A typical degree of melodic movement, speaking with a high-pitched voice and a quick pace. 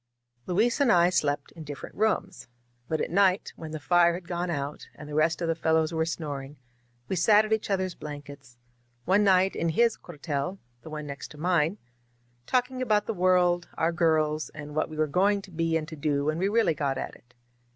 No: average, 3.8 semitones; medium, 165 Hz; fast, 225 wpm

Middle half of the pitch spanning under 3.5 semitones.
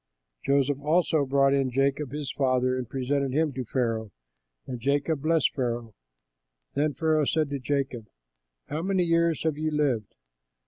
Yes: average, 3.0 semitones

